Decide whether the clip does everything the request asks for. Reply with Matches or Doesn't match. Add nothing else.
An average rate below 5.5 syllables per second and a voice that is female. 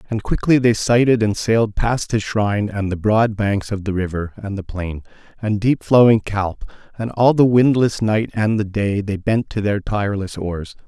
Doesn't match